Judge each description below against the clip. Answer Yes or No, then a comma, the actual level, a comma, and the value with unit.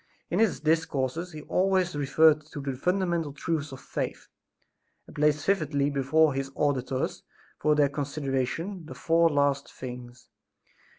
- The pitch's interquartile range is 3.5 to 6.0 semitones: No, average, 3.1 semitones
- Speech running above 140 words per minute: No, slow, 135 wpm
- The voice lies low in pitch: No, medium, 150 Hz